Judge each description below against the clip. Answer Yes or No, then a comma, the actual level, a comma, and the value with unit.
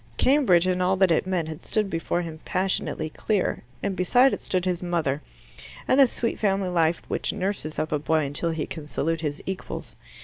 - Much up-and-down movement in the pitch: No, average, 3.2 semitones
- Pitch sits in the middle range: Yes, medium, 180 Hz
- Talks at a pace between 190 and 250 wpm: Yes, average, 200 wpm